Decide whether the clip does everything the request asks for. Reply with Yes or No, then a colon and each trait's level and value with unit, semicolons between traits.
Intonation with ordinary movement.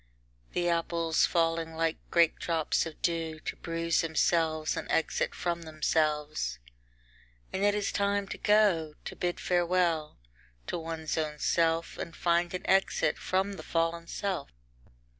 No: narrow, 1.6 semitones